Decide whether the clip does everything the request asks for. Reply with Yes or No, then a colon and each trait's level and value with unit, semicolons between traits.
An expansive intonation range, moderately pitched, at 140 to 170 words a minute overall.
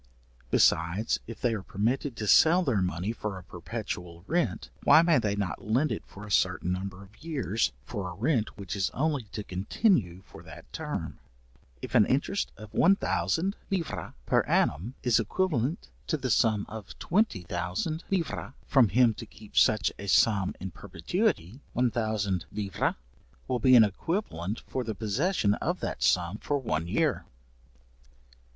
No: wide, 6.0 semitones; low, 110 Hz; average, 160 wpm